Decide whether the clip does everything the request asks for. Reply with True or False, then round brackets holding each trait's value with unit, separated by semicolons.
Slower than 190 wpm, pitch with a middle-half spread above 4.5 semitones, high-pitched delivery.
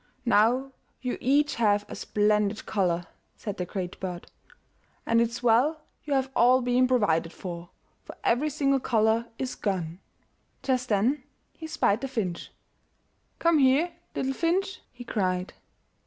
True (140 wpm; 5.0 semitones; 235 Hz)